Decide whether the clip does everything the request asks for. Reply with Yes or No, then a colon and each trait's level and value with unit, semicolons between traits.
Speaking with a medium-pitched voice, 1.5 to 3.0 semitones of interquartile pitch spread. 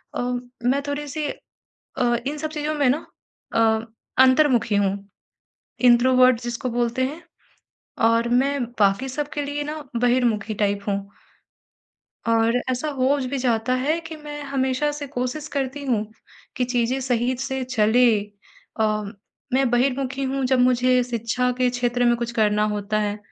No: very high, 250 Hz; average, 2.7 semitones